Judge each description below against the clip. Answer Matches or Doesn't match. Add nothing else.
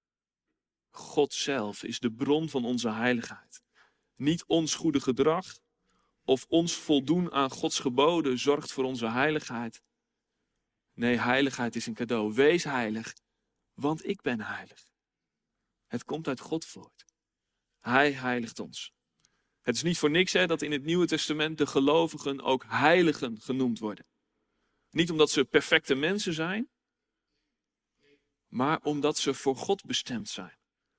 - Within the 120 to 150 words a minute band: Matches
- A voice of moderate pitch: Matches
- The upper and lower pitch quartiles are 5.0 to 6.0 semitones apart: Doesn't match